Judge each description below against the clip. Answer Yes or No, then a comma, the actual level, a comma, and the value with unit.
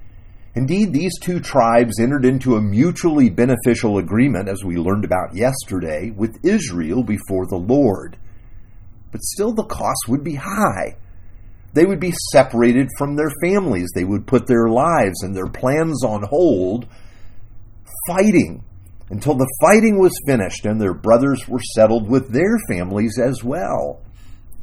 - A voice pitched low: Yes, low, 115 Hz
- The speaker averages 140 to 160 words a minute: Yes, average, 145 wpm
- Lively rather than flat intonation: Yes, wide, 6.0 semitones